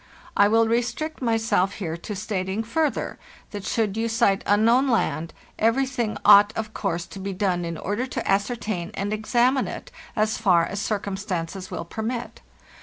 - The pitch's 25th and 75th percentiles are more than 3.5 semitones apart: No, average, 3.0 semitones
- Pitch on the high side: Yes, high, 210 Hz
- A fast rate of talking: No, average, 165 wpm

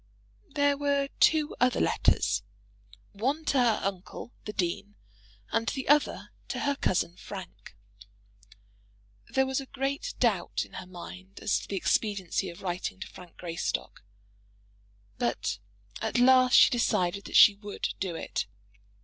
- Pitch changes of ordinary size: No, wide, 6.8 semitones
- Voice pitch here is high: Yes, high, 210 Hz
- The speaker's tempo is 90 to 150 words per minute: Yes, average, 140 wpm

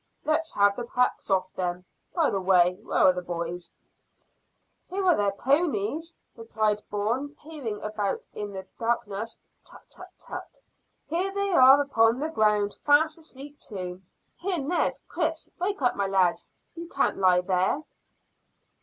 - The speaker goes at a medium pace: Yes, average, 150 wpm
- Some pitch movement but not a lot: No, wide, 8.1 semitones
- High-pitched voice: Yes, high, 225 Hz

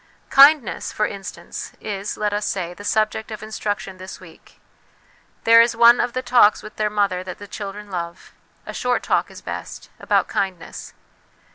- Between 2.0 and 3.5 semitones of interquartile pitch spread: Yes, average, 2.7 semitones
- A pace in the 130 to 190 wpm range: Yes, average, 170 wpm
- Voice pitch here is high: Yes, high, 210 Hz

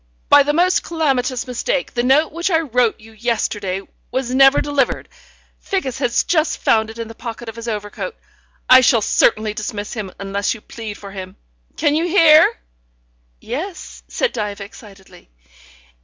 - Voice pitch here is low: No, high, 240 Hz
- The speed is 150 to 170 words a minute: Yes, average, 160 wpm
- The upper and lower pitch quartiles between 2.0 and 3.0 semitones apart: No, average, 5.3 semitones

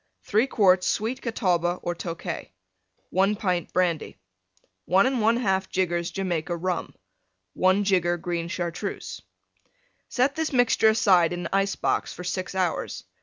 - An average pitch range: Yes, average, 3.3 semitones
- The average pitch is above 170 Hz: Yes, medium, 185 Hz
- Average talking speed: No, slow, 125 wpm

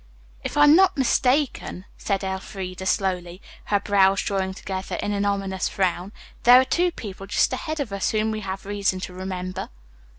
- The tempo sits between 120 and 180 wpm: Yes, average, 170 wpm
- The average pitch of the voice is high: Yes, high, 195 Hz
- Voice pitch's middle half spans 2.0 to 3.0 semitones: Yes, average, 2.7 semitones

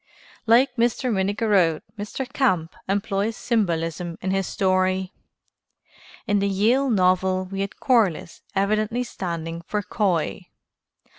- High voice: Yes, high, 195 Hz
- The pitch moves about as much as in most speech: Yes, average, 3.2 semitones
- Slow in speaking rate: Yes, slow, 115 wpm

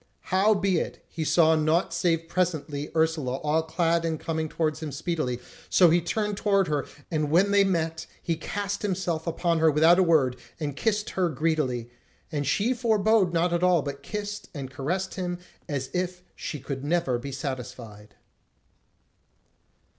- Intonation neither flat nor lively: Yes, average, 3.7 semitones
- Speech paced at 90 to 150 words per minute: No, average, 160 wpm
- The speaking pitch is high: No, medium, 165 Hz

